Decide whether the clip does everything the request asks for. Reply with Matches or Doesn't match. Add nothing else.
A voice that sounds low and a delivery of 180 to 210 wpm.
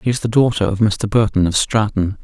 Doesn't match